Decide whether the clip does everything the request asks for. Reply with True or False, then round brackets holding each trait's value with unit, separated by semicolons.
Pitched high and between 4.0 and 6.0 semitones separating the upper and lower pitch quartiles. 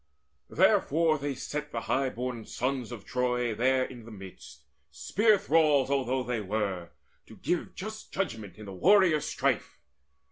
False (130 Hz; 5.3 semitones)